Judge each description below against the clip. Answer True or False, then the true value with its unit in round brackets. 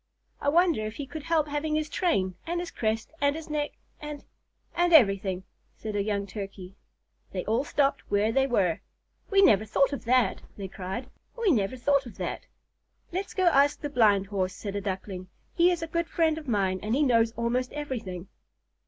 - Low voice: False (250 Hz)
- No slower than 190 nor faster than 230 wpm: True (195 wpm)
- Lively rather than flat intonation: True (7.1 semitones)